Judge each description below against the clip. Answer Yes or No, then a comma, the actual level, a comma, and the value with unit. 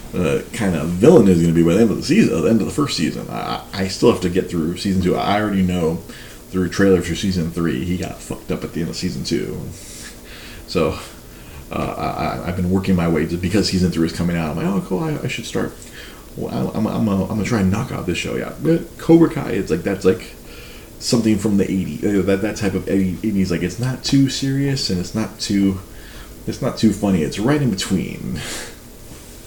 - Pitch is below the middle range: Yes, very low, 95 Hz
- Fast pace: Yes, fast, 240 wpm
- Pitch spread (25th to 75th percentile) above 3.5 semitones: Yes, average, 4.5 semitones